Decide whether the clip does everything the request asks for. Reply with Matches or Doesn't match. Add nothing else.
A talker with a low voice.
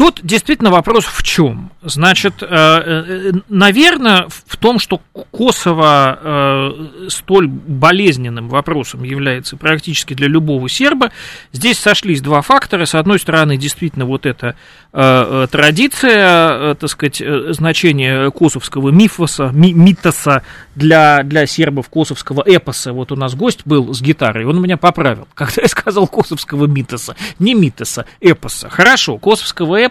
Doesn't match